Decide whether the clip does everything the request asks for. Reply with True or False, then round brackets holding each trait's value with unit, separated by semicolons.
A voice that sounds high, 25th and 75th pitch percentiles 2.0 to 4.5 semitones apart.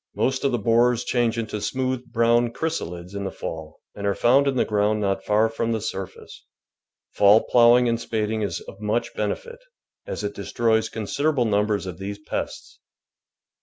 False (110 Hz; 3.0 semitones)